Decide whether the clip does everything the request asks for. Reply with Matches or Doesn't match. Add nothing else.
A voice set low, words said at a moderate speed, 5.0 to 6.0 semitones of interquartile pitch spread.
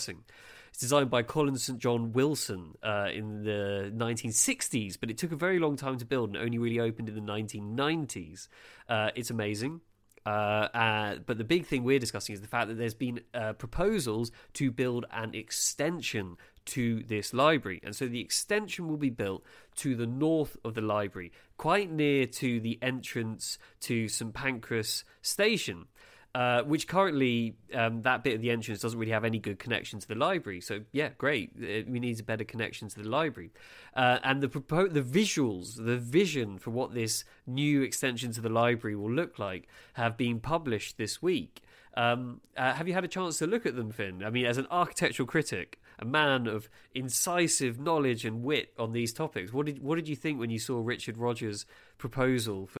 Doesn't match